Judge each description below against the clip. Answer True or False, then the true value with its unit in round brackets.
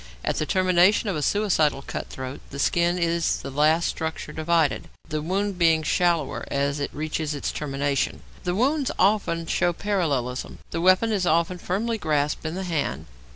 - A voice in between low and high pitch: True (165 Hz)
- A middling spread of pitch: True (3.7 semitones)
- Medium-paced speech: True (170 wpm)